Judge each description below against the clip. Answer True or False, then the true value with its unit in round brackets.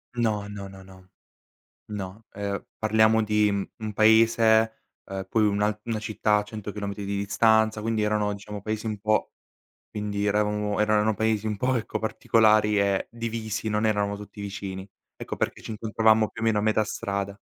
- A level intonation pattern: True (1.3 semitones)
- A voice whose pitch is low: True (105 Hz)